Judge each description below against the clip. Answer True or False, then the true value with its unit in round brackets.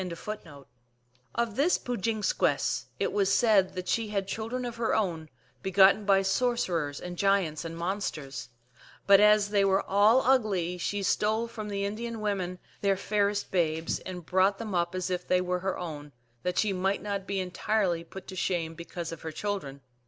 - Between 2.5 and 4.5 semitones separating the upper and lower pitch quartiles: True (3.0 semitones)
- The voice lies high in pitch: True (195 Hz)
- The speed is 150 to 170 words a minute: False (180 wpm)